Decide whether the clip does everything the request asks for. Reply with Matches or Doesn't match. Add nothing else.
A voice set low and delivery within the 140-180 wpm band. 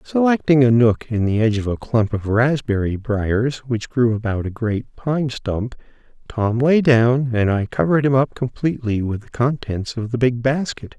Doesn't match